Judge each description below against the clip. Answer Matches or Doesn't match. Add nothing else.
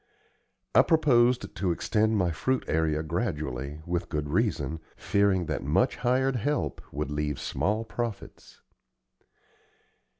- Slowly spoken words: Matches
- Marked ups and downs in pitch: Matches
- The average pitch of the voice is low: Matches